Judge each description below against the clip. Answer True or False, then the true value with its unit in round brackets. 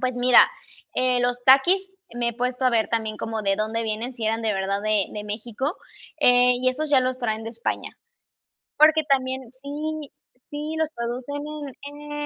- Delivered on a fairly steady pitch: False (3.5 semitones)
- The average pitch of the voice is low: False (245 Hz)